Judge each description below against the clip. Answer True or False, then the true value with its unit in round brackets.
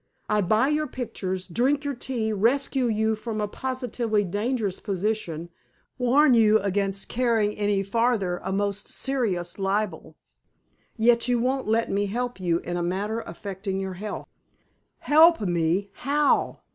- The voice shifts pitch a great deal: False (4.1 semitones)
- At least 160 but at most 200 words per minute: False (145 wpm)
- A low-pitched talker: False (215 Hz)